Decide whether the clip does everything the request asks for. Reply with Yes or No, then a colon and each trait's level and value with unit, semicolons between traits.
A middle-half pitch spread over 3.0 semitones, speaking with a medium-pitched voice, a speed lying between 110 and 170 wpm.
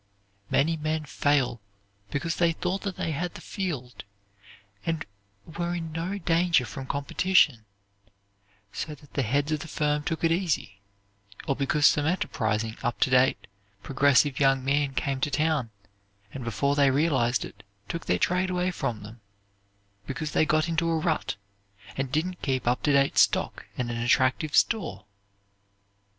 Yes: average, 3.9 semitones; medium, 145 Hz; average, 155 wpm